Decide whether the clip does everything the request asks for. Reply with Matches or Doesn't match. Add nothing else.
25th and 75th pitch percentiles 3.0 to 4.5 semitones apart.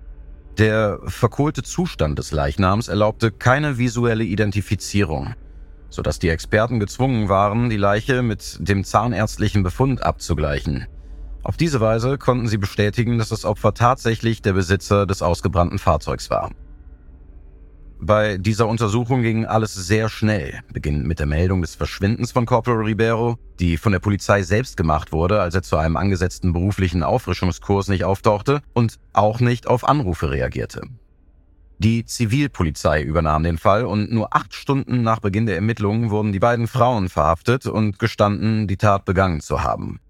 Doesn't match